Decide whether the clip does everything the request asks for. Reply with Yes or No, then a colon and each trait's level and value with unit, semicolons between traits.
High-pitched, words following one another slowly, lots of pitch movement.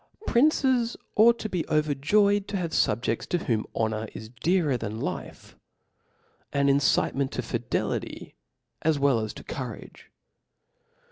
No: medium, 150 Hz; slow, 130 wpm; wide, 9.0 semitones